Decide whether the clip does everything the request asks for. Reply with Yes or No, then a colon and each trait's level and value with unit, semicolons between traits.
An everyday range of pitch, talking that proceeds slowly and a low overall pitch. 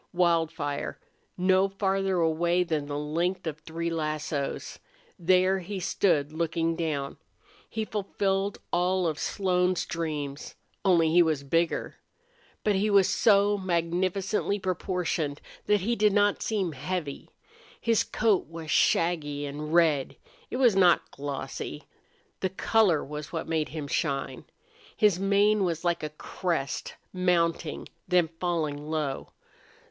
No: average, 3.6 semitones; slow, 130 wpm; medium, 170 Hz